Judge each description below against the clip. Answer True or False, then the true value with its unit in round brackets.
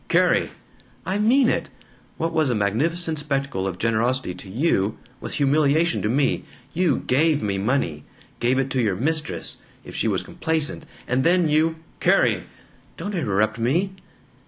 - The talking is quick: False (160 wpm)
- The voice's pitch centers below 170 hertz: True (140 Hz)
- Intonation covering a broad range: True (6.8 semitones)